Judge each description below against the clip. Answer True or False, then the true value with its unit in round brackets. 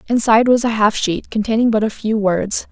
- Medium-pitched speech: False (220 Hz)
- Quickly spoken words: True (220 wpm)